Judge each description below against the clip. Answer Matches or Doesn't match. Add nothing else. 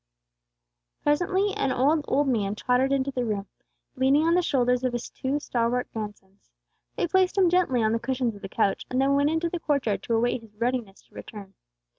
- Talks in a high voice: Matches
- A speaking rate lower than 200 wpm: Doesn't match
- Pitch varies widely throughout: Doesn't match